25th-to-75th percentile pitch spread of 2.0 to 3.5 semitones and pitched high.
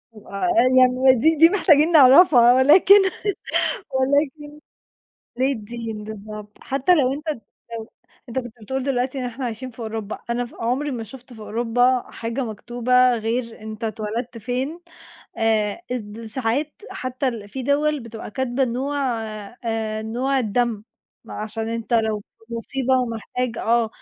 Yes: average, 3.0 semitones; high, 245 Hz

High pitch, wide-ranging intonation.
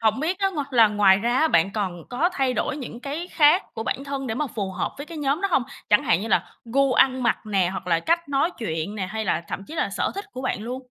Yes: very high, 250 Hz; wide, 5.9 semitones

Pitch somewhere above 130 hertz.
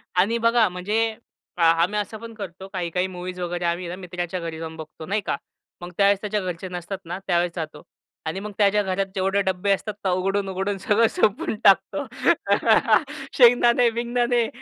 Yes: high, 190 Hz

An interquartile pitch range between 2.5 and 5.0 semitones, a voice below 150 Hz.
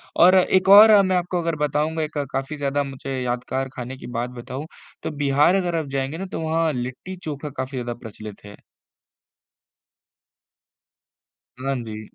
Yes: average, 4.7 semitones; medium, 140 Hz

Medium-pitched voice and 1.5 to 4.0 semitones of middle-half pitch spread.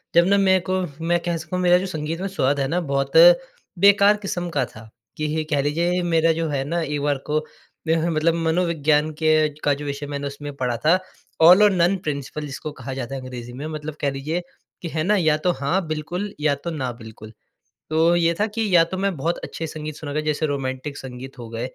Yes: medium, 155 Hz; average, 3.5 semitones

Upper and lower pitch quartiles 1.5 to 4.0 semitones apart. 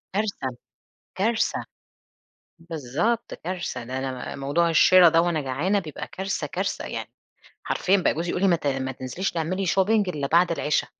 No: average, 5.2 semitones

